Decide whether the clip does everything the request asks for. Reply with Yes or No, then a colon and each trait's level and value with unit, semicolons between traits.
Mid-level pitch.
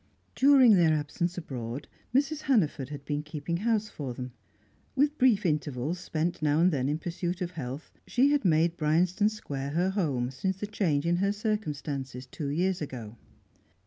Yes: medium, 165 Hz